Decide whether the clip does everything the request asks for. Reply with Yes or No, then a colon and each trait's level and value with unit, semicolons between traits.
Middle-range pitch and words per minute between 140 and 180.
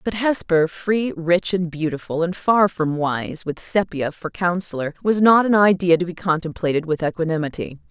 Yes: medium, 175 Hz; average, 175 wpm